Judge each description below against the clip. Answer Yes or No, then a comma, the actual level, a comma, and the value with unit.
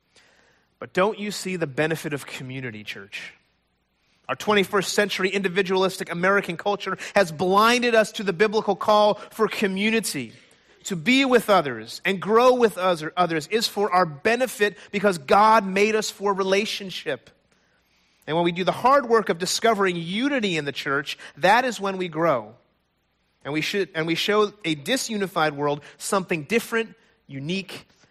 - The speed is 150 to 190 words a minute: Yes, average, 160 wpm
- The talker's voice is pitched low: No, high, 195 Hz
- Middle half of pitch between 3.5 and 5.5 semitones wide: Yes, average, 4.2 semitones